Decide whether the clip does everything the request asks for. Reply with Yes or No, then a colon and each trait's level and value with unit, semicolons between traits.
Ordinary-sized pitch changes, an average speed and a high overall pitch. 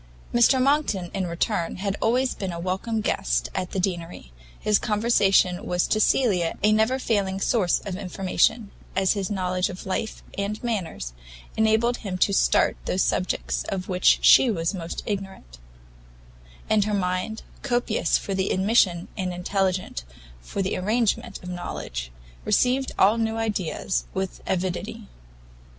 Yes: average, 3.3 semitones; average, 145 wpm; high, 195 Hz